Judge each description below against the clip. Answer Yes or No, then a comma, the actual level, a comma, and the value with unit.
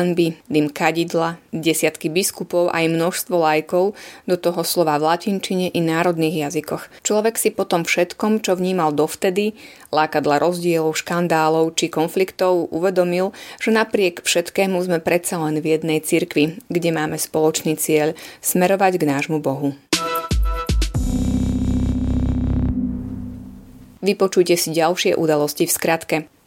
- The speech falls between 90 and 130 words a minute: Yes, average, 120 wpm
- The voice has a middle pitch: Yes, medium, 165 Hz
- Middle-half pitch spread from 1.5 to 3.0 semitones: Yes, average, 2.7 semitones